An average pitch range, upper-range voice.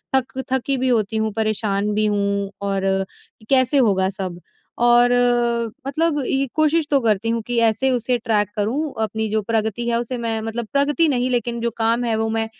Yes: average, 3.1 semitones; high, 230 Hz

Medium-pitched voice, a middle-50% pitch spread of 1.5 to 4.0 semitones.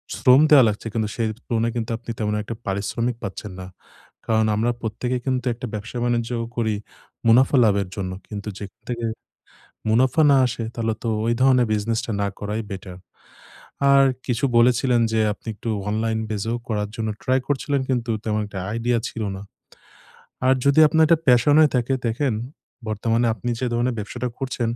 No: low, 115 Hz; narrow, 2.6 semitones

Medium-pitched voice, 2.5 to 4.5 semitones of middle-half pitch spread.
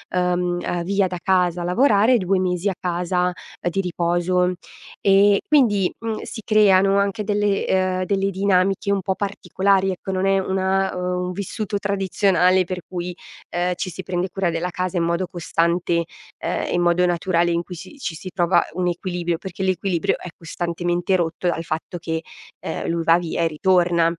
No: medium, 180 Hz; narrow, 1.9 semitones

